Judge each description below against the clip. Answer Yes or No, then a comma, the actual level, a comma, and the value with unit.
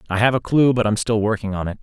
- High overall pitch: No, low, 110 Hz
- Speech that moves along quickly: Yes, fast, 330 wpm